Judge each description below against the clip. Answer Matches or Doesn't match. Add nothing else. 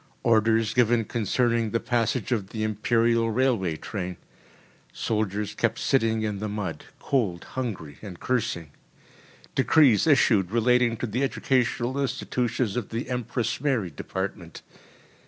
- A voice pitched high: Doesn't match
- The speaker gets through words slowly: Matches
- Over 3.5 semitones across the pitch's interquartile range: Doesn't match